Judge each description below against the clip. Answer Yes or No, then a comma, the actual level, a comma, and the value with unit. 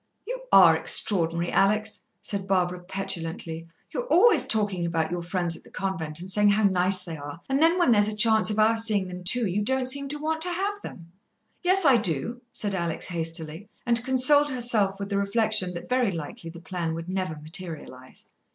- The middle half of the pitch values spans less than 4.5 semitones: No, wide, 5.6 semitones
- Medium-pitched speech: No, high, 195 Hz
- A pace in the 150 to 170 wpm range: No, average, 195 wpm